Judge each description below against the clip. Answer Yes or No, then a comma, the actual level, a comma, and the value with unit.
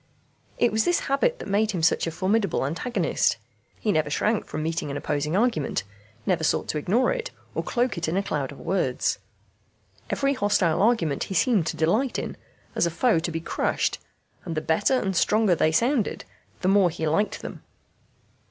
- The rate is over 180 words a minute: Yes, average, 190 wpm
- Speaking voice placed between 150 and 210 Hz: Yes, medium, 185 Hz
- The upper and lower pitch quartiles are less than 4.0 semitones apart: No, wide, 5.6 semitones